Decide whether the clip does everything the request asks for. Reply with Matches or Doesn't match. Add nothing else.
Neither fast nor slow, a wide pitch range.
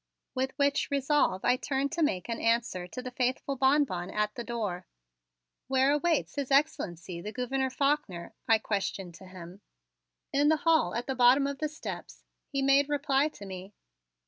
Matches